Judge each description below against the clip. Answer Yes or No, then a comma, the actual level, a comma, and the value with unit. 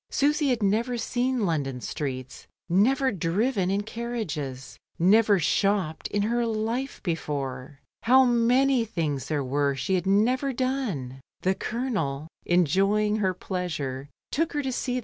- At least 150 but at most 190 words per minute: No, slow, 135 wpm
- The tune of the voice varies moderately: No, wide, 8.1 semitones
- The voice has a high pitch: Yes, high, 200 Hz